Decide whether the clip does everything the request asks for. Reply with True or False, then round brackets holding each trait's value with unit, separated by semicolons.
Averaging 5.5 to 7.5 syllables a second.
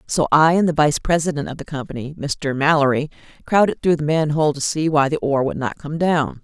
True (5.8 syllables/s)